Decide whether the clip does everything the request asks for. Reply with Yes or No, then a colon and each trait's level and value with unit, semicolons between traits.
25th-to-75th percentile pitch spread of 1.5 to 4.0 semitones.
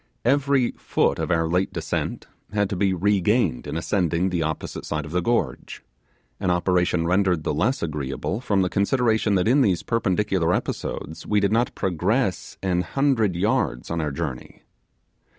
No: average, 4.4 semitones